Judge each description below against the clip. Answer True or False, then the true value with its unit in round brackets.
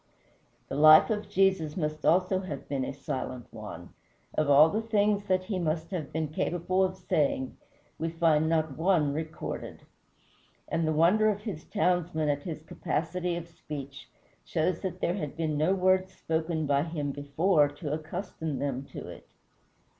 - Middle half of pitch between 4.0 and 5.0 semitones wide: False (3.6 semitones)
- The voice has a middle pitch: True (160 Hz)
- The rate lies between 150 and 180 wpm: True (165 wpm)